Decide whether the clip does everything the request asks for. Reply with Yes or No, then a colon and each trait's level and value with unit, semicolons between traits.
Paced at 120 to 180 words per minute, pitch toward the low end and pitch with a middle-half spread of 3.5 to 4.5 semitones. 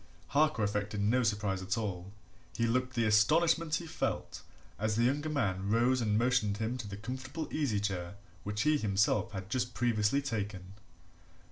Yes: average, 165 wpm; low, 110 Hz; average, 3.9 semitones